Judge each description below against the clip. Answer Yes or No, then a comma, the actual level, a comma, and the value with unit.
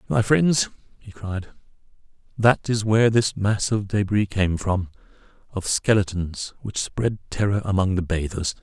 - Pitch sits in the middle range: No, low, 100 Hz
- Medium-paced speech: No, slow, 130 wpm